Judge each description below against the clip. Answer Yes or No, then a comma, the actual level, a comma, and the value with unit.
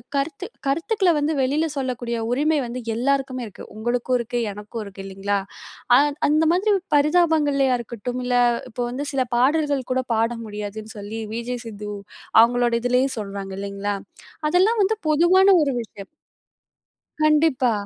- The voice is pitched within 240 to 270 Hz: Yes, very high, 250 Hz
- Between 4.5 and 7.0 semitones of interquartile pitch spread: Yes, average, 5.2 semitones